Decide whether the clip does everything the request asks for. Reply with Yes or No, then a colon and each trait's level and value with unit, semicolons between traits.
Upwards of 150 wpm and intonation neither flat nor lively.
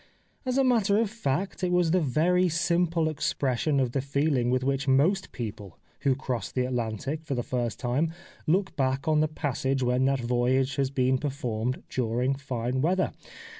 Yes: average, 175 wpm; average, 4.3 semitones